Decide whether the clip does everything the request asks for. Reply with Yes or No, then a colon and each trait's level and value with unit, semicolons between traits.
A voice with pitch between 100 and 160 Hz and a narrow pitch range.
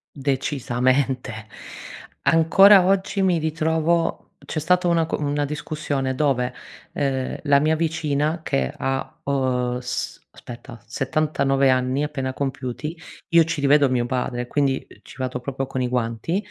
No: medium, 140 Hz; average, 3.5 semitones